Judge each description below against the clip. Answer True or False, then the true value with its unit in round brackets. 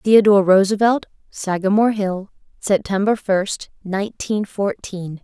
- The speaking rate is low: True (90 wpm)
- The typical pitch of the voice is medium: False (200 Hz)